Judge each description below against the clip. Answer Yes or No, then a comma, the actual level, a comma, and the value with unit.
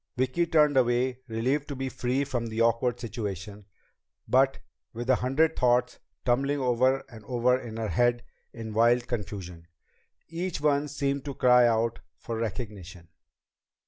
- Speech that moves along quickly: No, average, 145 wpm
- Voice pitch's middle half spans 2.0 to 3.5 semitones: Yes, average, 2.8 semitones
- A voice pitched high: No, low, 125 Hz